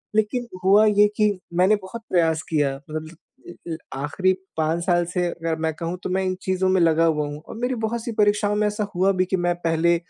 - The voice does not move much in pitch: No, average, 4.1 semitones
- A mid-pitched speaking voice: Yes, medium, 180 Hz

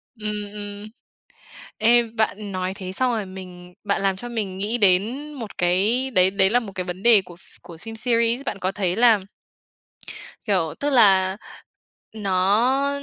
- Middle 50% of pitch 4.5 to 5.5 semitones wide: No, average, 3.7 semitones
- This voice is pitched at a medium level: No, high, 205 Hz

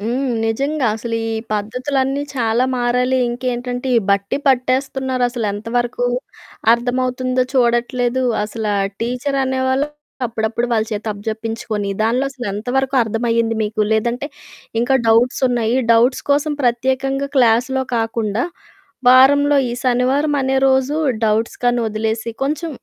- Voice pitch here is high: Yes, high, 245 Hz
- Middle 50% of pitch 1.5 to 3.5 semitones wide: Yes, narrow, 2.6 semitones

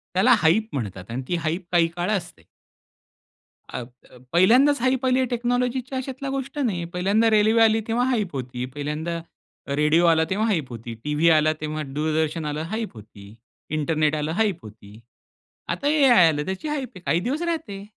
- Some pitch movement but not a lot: No, wide, 8.0 semitones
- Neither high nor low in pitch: Yes, medium, 180 Hz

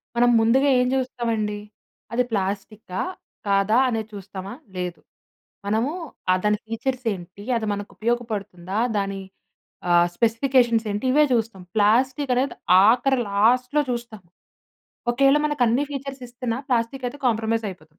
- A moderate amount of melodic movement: Yes, average, 3.6 semitones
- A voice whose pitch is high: Yes, high, 230 Hz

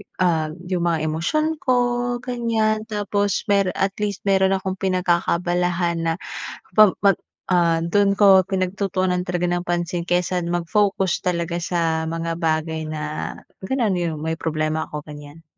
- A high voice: No, medium, 175 Hz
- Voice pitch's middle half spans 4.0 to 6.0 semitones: No, average, 2.9 semitones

